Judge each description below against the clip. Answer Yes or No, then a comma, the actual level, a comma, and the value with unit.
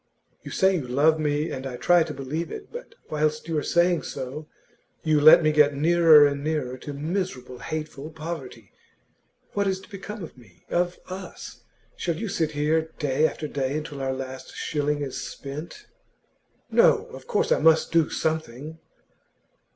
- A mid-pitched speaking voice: Yes, medium, 155 Hz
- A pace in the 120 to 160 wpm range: No, average, 170 wpm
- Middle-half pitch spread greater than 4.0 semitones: No, average, 2.9 semitones